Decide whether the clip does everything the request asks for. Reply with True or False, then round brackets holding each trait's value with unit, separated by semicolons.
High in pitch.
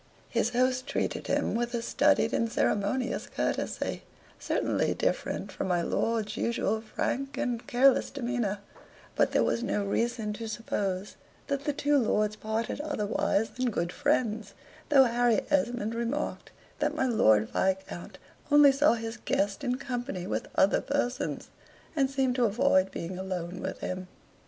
True (235 Hz)